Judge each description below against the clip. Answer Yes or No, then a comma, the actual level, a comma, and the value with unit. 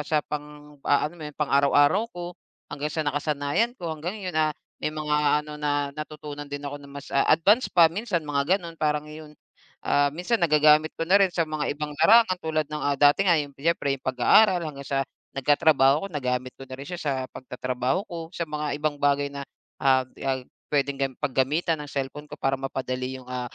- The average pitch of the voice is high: No, medium, 150 Hz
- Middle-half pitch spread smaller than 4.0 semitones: Yes, narrow, 2.4 semitones